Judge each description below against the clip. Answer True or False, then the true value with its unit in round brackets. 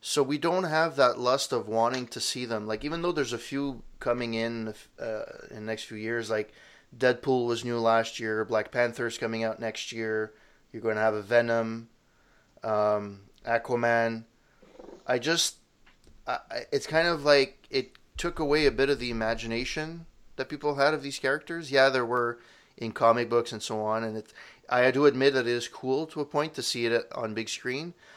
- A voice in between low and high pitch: False (120 Hz)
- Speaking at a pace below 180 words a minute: False (200 wpm)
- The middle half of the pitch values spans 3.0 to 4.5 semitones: True (3.7 semitones)